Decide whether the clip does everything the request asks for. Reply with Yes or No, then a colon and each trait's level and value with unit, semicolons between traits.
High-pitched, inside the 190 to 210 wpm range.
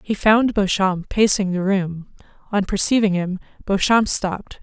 No: high, 195 Hz; average, 145 wpm